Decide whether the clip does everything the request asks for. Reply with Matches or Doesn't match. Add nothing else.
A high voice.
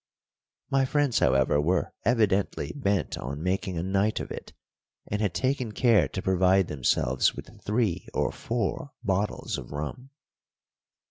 Doesn't match